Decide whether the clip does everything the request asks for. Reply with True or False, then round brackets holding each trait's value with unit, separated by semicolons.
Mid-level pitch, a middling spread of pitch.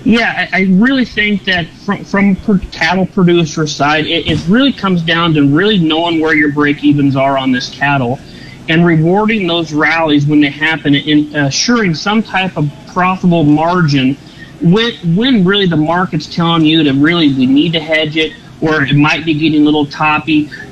True (160 Hz; 3.6 semitones)